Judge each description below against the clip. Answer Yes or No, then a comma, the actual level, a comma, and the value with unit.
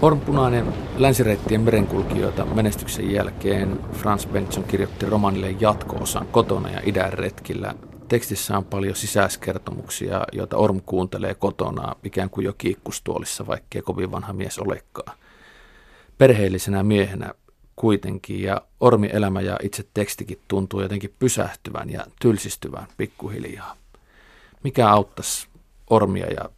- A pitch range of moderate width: No, narrow, 2.0 semitones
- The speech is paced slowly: No, average, 115 wpm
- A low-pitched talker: Yes, low, 100 Hz